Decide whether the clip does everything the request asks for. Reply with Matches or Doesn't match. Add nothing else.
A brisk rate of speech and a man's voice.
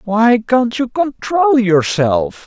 Doesn't match